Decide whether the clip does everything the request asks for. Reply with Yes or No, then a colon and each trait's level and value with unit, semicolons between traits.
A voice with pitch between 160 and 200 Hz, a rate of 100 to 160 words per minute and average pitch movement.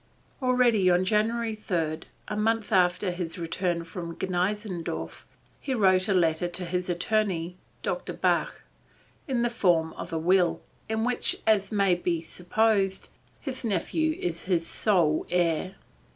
Yes: medium, 185 Hz; average, 140 wpm; average, 3.8 semitones